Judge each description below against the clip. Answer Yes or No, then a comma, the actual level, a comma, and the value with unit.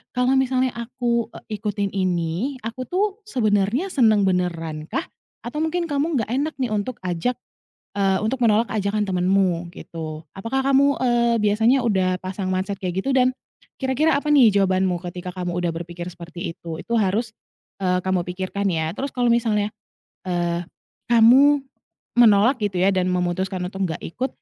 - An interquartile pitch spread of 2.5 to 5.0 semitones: No, wide, 5.4 semitones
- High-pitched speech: Yes, high, 205 Hz